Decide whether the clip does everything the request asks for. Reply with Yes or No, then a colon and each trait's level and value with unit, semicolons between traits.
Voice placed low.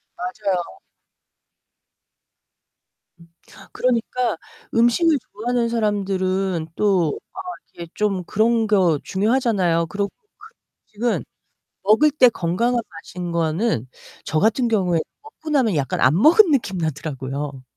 No: high, 200 Hz